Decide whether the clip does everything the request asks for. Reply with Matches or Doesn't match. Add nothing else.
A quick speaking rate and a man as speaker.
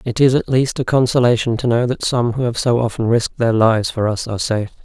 Matches